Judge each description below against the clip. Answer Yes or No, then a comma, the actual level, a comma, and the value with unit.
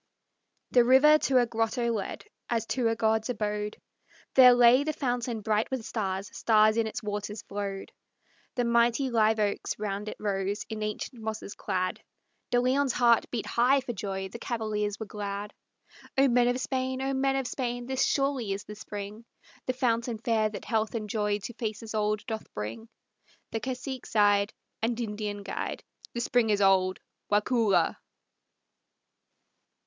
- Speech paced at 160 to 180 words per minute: Yes, average, 165 wpm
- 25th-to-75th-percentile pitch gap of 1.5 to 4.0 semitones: Yes, average, 2.9 semitones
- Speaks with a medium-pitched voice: No, high, 225 Hz